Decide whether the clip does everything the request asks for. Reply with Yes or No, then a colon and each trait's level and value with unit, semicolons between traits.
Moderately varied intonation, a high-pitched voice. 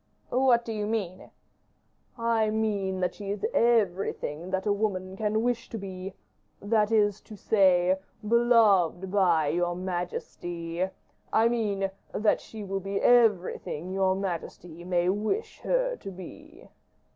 Yes: average, 3.2 semitones; high, 195 Hz